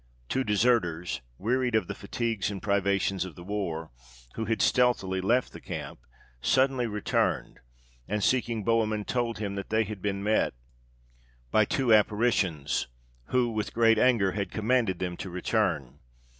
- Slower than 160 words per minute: Yes, average, 150 wpm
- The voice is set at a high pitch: No, low, 105 Hz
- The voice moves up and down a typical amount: Yes, average, 3.3 semitones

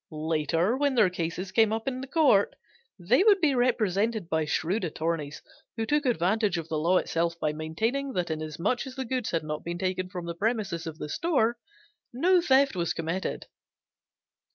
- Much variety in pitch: Yes, wide, 7.0 semitones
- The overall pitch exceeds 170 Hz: Yes, high, 190 Hz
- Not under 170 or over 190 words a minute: Yes, average, 175 wpm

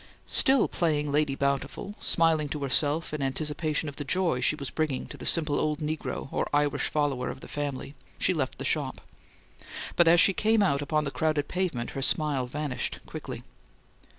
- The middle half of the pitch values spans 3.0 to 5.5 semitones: No, narrow, 2.4 semitones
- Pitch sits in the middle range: Yes, medium, 150 Hz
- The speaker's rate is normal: Yes, average, 180 wpm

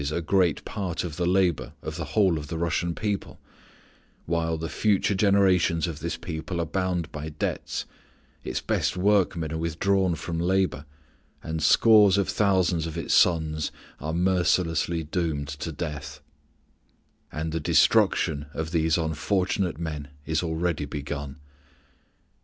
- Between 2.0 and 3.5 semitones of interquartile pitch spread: Yes, average, 2.8 semitones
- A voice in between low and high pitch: No, very low, 85 Hz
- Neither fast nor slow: Yes, average, 145 wpm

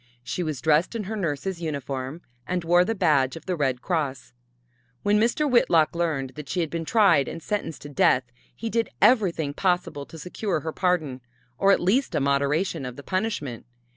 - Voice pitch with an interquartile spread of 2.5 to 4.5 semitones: No, average, 5.3 semitones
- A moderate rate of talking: Yes, average, 190 wpm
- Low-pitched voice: No, medium, 165 Hz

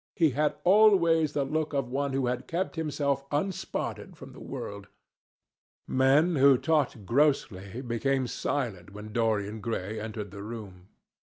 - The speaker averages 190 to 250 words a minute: No, average, 145 wpm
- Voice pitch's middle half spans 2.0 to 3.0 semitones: No, wide, 5.6 semitones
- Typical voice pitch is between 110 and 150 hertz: Yes, low, 135 Hz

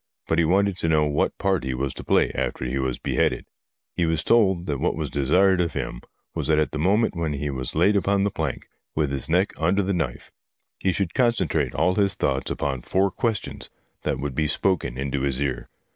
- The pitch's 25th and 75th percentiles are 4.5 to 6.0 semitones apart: Yes, wide, 5.5 semitones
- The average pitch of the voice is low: Yes, very low, 80 Hz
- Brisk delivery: Yes, fast, 220 wpm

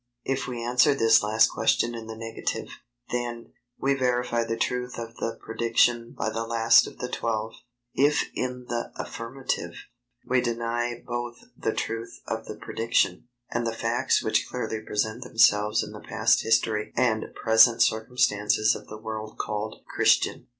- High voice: No, low, 115 Hz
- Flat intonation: Yes, narrow, 1.5 semitones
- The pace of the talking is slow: No, average, 155 wpm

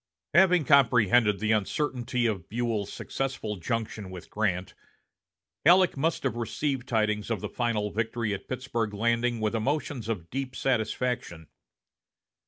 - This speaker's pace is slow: Yes, slow, 130 wpm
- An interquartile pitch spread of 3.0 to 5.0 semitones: Yes, average, 3.5 semitones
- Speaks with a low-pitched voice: Yes, low, 115 Hz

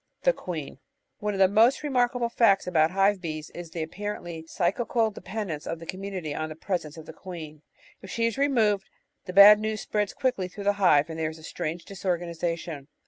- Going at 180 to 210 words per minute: Yes, average, 200 wpm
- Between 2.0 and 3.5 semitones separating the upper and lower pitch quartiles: No, average, 4.4 semitones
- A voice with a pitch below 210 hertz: Yes, medium, 185 Hz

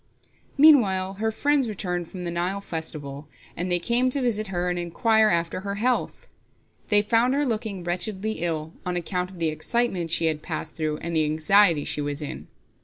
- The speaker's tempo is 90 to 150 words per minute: No, average, 185 wpm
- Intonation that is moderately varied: Yes, average, 4.6 semitones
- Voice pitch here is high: No, medium, 180 Hz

